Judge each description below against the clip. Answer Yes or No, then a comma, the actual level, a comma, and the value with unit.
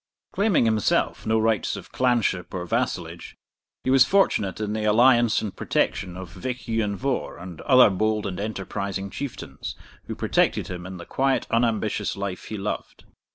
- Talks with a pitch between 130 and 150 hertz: No, low, 110 Hz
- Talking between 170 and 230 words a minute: No, average, 160 wpm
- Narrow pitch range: No, average, 3.9 semitones